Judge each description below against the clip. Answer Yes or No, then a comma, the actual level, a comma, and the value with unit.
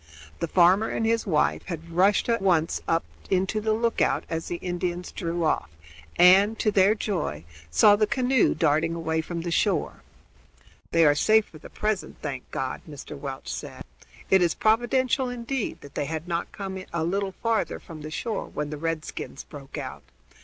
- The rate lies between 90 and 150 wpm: No, average, 175 wpm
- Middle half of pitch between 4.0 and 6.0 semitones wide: Yes, average, 5.0 semitones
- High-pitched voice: No, medium, 175 Hz